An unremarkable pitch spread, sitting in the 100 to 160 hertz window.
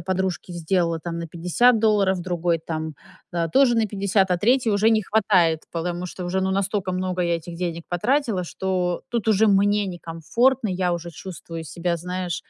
No: average, 3.1 semitones; medium, 185 Hz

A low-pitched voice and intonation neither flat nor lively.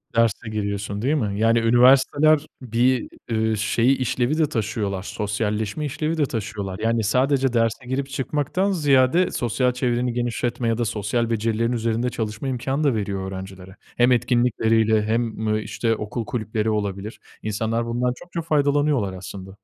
Yes: low, 115 Hz; average, 3.2 semitones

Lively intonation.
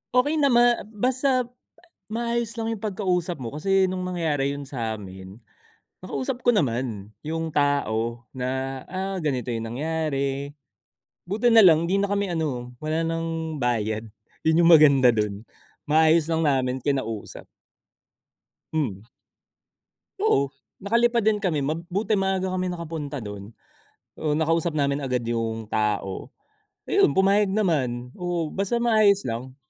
Yes: wide, 7.1 semitones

